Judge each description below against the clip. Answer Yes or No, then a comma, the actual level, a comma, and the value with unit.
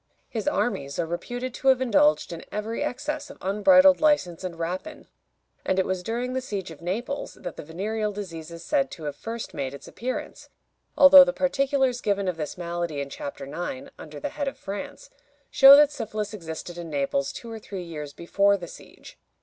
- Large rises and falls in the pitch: Yes, wide, 7.6 semitones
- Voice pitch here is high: Yes, high, 200 Hz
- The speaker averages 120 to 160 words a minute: No, average, 195 wpm